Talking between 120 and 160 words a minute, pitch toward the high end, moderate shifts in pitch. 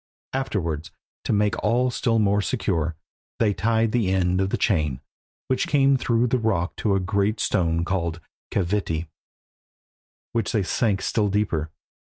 No: average, 150 wpm; low, 100 Hz; average, 4.3 semitones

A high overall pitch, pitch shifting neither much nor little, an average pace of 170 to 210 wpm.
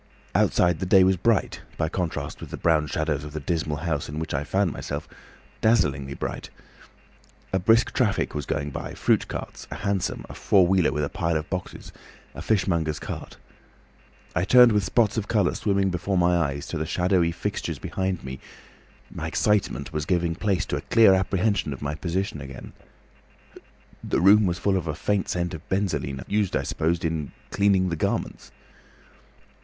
No: very low, 90 Hz; average, 4.0 semitones; average, 180 wpm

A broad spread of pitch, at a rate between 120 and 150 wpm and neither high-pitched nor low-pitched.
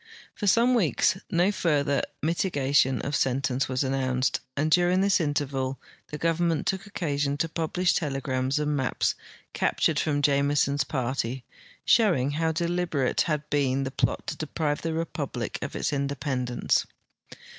No: average, 3.7 semitones; average, 145 wpm; medium, 145 Hz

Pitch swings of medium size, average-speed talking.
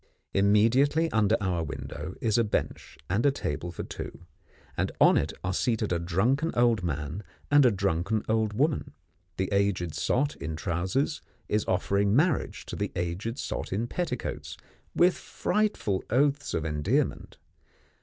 No: wide, 6.0 semitones; average, 145 wpm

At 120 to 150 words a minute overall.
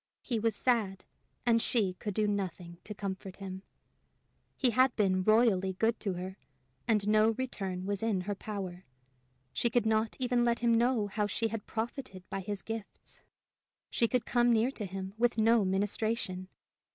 No: average, 165 wpm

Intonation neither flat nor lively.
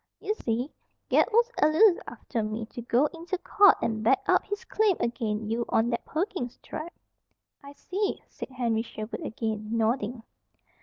No: wide, 7.4 semitones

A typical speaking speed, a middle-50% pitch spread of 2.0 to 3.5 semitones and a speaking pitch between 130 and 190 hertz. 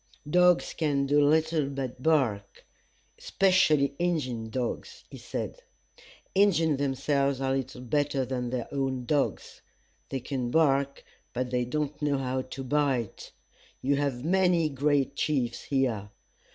No: slow, 130 wpm; average, 2.8 semitones; medium, 140 Hz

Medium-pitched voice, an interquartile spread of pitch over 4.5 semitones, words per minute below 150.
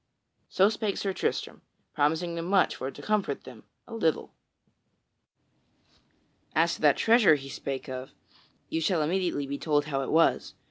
No: medium, 160 Hz; average, 4.9 semitones; average, 155 wpm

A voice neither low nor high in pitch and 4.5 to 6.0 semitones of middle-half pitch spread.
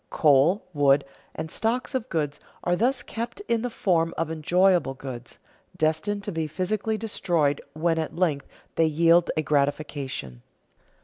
Yes: medium, 165 Hz; wide, 5.6 semitones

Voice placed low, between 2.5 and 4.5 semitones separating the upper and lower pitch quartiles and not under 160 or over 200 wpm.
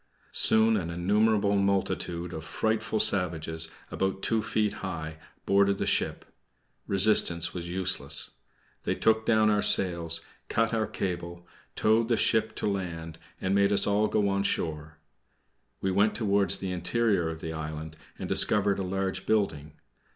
No: very low, 95 Hz; average, 3.7 semitones; average, 150 wpm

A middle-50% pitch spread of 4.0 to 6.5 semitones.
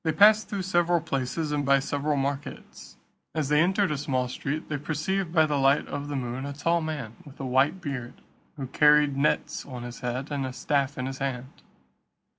No: average, 2.8 semitones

